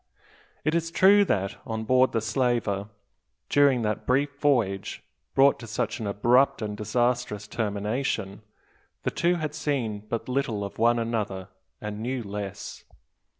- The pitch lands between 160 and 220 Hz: No, low, 115 Hz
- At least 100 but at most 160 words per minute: Yes, average, 145 wpm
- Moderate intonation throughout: Yes, average, 4.6 semitones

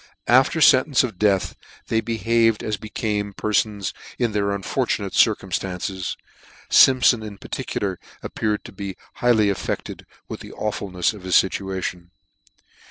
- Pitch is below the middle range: Yes, low, 105 Hz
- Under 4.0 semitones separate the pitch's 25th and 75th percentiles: Yes, average, 2.9 semitones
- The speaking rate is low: Yes, slow, 130 wpm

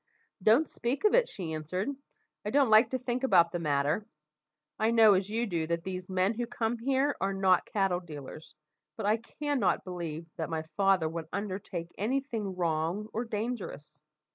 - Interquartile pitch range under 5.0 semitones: No, average, 5.3 semitones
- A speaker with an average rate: Yes, average, 180 wpm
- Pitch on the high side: Yes, high, 195 Hz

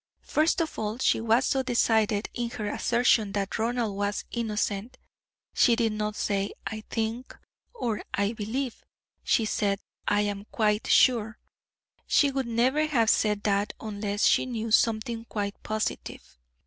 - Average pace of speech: Yes, average, 150 wpm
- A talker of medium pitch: No, high, 220 Hz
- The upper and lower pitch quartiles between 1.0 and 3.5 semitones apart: Yes, narrow, 2.5 semitones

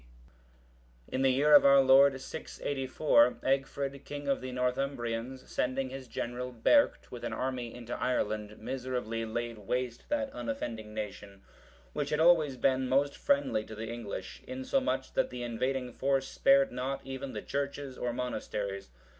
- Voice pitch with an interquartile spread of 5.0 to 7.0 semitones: No, average, 2.7 semitones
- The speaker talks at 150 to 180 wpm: Yes, average, 155 wpm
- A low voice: Yes, low, 130 Hz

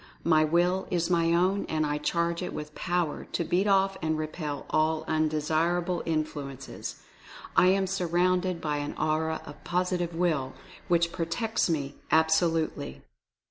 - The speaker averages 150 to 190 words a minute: No, average, 140 wpm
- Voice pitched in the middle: Yes, medium, 165 Hz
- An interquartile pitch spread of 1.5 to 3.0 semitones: Yes, narrow, 2.4 semitones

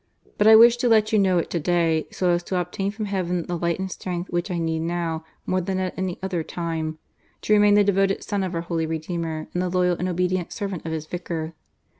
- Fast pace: Yes, fast, 240 wpm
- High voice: No, medium, 180 Hz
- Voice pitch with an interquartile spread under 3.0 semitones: Yes, narrow, 2.4 semitones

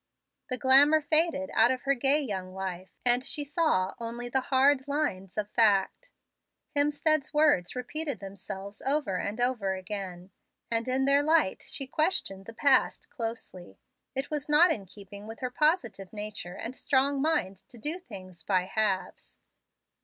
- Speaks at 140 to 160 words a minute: Yes, average, 155 wpm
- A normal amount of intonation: No, wide, 6.6 semitones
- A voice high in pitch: Yes, high, 245 Hz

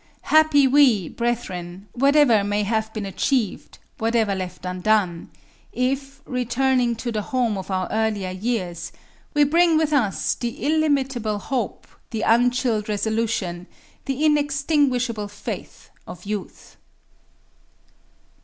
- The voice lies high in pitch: Yes, high, 230 Hz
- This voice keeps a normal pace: No, slow, 115 wpm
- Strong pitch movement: No, average, 4.9 semitones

